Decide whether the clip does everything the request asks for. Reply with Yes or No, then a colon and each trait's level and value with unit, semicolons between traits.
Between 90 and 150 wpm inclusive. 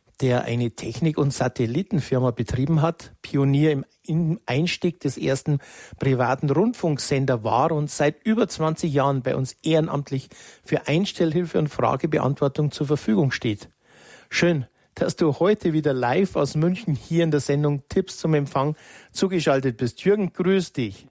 Yes: average, 140 wpm